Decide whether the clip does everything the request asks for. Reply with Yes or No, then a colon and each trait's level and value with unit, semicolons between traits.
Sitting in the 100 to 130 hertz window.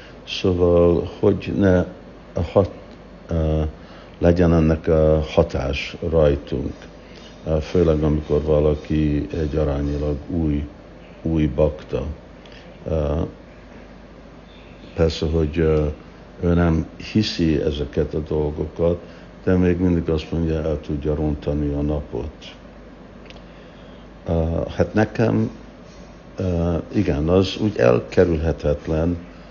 No: very low, 80 Hz